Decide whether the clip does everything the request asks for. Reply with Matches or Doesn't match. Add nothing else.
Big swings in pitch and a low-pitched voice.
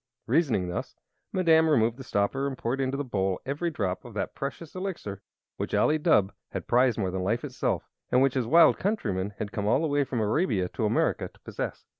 Matches